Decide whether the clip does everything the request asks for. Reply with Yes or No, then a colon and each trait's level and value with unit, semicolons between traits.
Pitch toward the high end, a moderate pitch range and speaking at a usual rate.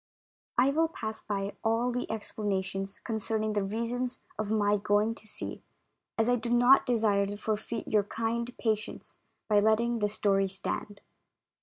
No: high, 220 Hz; narrow, 2.3 semitones; average, 160 wpm